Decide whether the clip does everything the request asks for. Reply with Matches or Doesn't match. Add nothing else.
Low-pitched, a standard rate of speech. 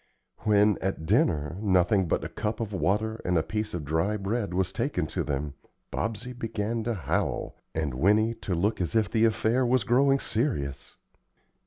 Matches